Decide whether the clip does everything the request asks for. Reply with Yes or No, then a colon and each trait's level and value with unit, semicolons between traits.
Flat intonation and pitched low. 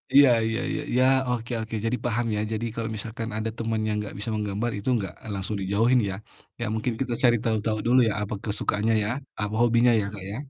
Yes: narrow, 2.2 semitones; low, 110 Hz